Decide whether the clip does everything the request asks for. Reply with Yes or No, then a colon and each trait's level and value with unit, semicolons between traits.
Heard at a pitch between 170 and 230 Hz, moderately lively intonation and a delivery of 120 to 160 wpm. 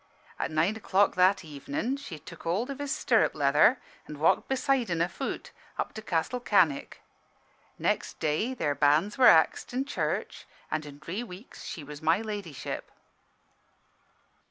No: medium, 185 Hz; wide, 7.0 semitones; average, 155 wpm